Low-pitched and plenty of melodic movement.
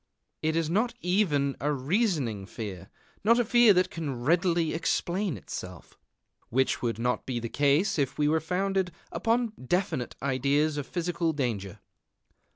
No: medium, 155 Hz; wide, 5.7 semitones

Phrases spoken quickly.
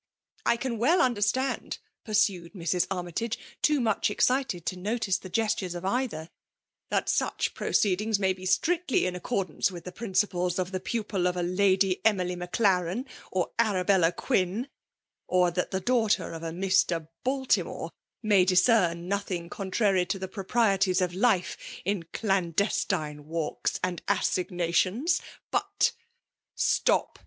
No: average, 155 wpm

